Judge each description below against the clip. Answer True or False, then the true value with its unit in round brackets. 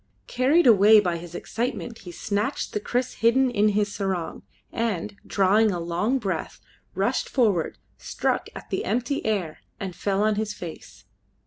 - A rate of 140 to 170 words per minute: True (155 wpm)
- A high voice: True (210 Hz)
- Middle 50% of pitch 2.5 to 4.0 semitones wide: True (3.7 semitones)